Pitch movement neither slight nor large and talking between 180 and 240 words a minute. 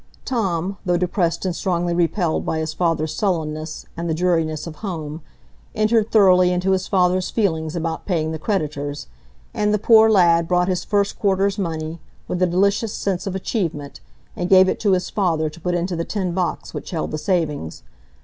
Yes: average, 3.1 semitones; average, 185 wpm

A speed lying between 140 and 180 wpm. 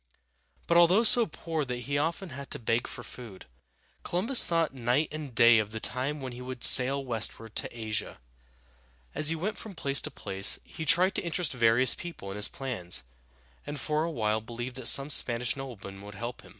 No: average, 195 wpm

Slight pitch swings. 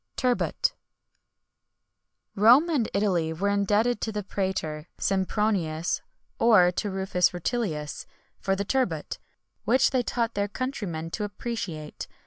No: average, 4.6 semitones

